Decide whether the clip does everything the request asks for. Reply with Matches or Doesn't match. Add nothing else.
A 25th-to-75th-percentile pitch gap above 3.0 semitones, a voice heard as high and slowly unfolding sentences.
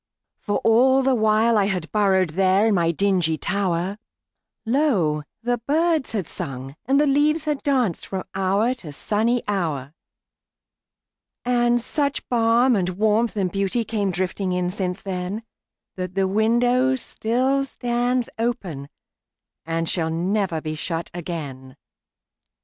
Matches